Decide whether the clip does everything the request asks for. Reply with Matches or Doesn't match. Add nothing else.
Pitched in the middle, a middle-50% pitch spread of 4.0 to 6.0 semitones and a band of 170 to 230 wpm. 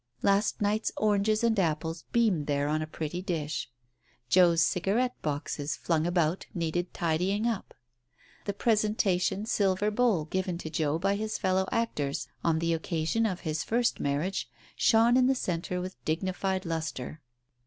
Doesn't match